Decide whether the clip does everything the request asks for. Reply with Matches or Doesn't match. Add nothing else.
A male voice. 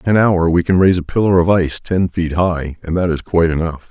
Matches